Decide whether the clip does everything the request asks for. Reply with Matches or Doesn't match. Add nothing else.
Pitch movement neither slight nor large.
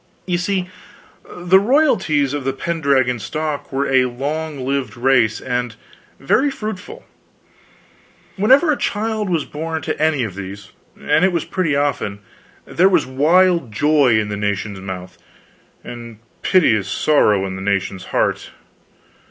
Doesn't match